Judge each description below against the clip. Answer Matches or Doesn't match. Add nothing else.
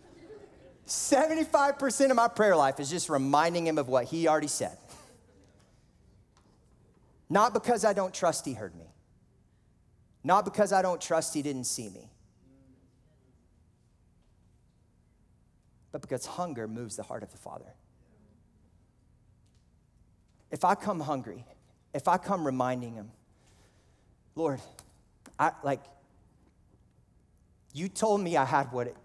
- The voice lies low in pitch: Doesn't match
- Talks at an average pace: Doesn't match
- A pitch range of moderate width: Doesn't match